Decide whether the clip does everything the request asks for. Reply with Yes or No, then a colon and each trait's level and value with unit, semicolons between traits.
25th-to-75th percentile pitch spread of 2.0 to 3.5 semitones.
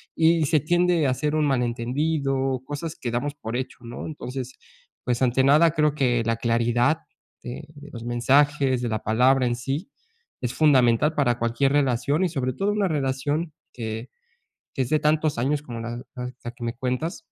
No: average, 3.9 semitones